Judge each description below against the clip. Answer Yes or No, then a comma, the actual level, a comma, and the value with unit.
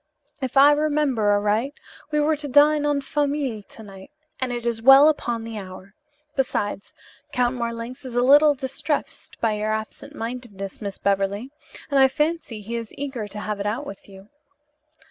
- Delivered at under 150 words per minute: No, average, 175 wpm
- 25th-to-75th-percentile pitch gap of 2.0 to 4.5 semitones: No, average, 5.1 semitones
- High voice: Yes, high, 240 Hz